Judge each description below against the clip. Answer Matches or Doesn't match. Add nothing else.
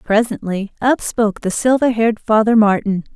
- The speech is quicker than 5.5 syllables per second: Doesn't match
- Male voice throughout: Doesn't match